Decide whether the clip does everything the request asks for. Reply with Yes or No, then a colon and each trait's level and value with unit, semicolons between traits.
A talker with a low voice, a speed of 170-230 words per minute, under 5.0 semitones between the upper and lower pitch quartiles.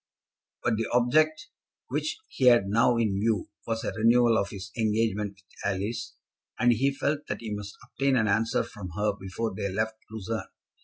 Yes: low, 110 Hz; average, 175 wpm; average, 2.9 semitones